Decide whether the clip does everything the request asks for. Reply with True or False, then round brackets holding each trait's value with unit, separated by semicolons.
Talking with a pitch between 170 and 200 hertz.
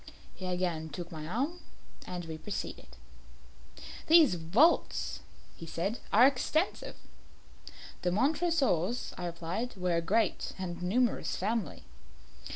True (185 Hz)